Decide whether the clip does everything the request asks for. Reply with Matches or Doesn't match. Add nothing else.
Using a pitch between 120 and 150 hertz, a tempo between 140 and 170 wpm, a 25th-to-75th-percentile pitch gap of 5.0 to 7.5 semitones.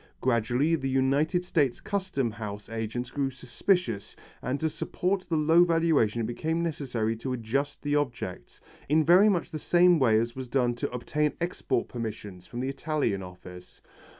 Matches